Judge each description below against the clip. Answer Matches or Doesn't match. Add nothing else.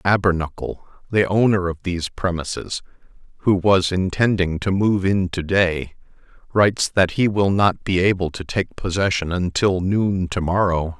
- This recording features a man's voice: Matches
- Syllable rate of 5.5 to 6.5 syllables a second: Doesn't match